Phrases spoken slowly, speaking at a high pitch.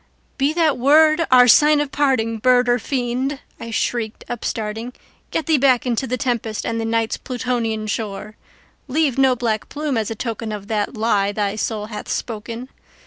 No: average, 165 wpm; high, 235 Hz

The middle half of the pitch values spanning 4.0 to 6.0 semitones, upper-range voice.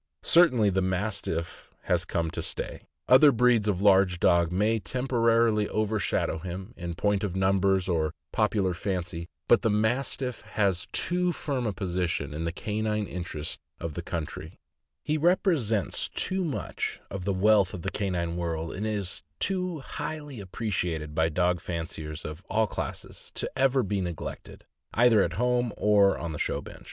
No: average, 4.7 semitones; low, 100 Hz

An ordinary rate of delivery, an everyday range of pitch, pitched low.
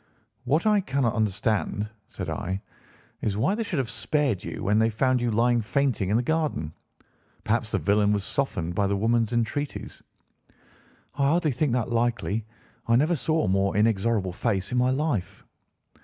Yes: average, 170 wpm; average, 4.8 semitones; low, 115 Hz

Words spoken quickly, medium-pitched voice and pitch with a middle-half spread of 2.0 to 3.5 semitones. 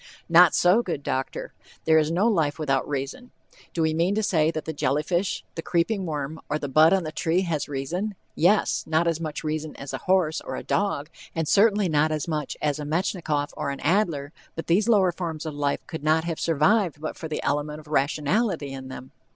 Yes: fast, 215 wpm; medium, 160 Hz; average, 3.2 semitones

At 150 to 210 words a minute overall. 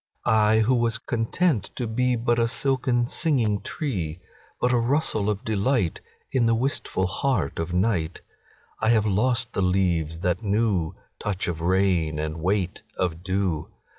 No: slow, 135 wpm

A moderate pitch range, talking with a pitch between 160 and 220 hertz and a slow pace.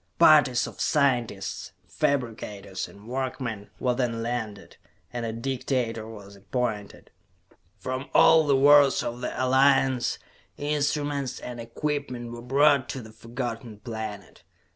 No: average, 3.2 semitones; low, 125 Hz; slow, 120 wpm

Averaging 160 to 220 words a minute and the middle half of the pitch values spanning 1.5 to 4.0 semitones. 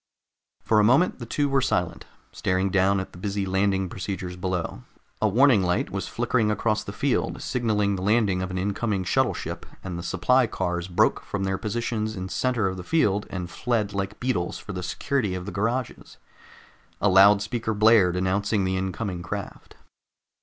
Yes: average, 180 wpm; average, 3.0 semitones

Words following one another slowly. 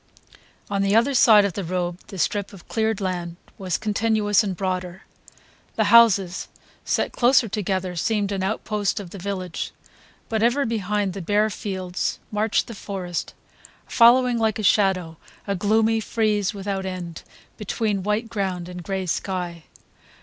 No: average, 150 wpm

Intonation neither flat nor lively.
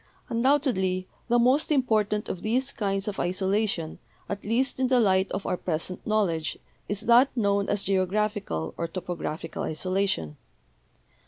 Yes: average, 3.9 semitones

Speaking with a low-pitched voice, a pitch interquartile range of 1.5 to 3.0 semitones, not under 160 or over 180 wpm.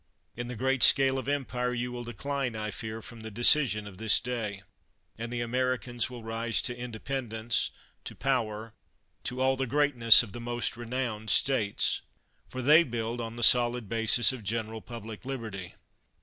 Yes: low, 120 Hz; narrow, 2.4 semitones; average, 170 wpm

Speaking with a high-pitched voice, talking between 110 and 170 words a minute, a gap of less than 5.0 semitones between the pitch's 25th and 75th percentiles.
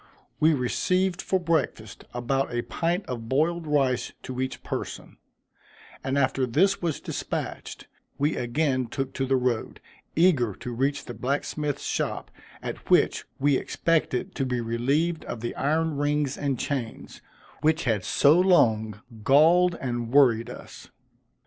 No: low, 135 Hz; average, 145 wpm; average, 4.4 semitones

